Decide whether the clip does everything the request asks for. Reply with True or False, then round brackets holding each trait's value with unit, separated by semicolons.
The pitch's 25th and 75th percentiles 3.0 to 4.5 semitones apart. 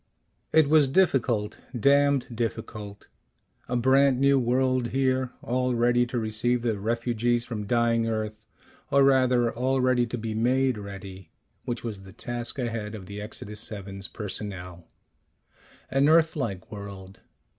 True (3.4 semitones)